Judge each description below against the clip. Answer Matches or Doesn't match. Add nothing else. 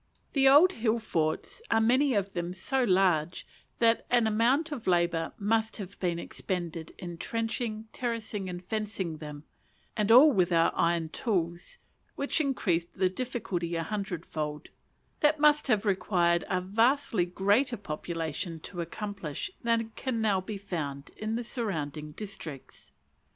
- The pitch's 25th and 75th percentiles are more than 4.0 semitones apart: Matches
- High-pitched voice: Matches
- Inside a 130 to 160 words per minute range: Matches